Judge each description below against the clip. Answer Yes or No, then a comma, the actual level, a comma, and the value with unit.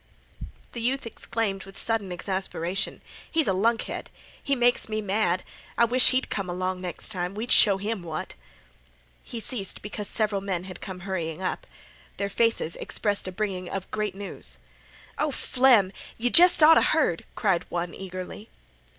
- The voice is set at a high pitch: Yes, high, 200 Hz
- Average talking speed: Yes, average, 160 wpm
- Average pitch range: Yes, average, 3.7 semitones